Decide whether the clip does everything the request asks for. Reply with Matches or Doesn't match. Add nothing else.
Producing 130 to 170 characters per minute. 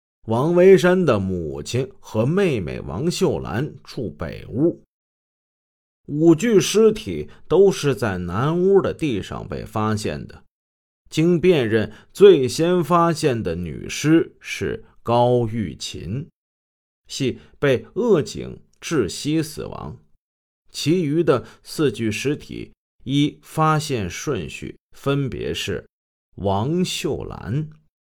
Matches